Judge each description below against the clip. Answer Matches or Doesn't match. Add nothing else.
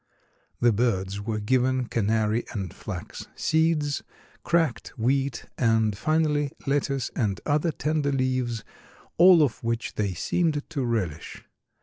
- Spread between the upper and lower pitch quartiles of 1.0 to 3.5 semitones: Doesn't match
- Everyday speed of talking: Doesn't match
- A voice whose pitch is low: Matches